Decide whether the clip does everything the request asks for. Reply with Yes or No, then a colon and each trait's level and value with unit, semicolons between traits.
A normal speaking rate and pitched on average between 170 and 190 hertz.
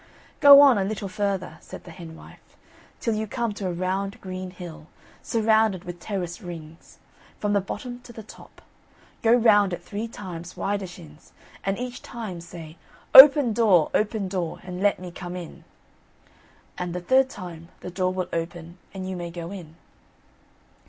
Yes: average, 170 wpm; medium, 185 Hz